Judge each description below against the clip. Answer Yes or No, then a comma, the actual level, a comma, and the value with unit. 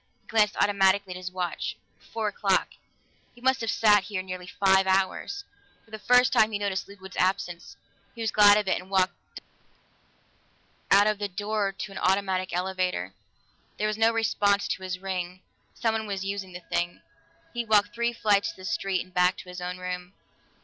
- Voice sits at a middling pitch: No, high, 195 Hz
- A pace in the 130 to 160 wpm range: No, average, 190 wpm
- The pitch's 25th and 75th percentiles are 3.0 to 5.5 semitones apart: No, narrow, 2.4 semitones